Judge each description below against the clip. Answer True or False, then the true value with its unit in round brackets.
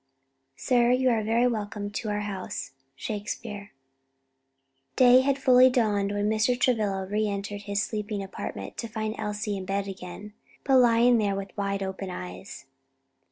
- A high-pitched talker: True (210 Hz)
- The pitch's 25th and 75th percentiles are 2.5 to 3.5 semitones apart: True (2.8 semitones)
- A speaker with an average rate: True (155 wpm)